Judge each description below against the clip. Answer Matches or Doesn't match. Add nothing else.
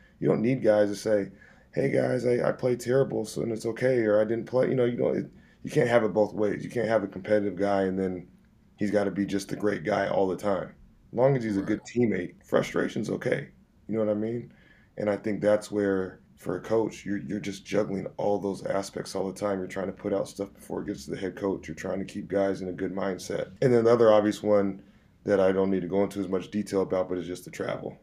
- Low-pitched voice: Matches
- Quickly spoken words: Matches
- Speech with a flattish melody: Matches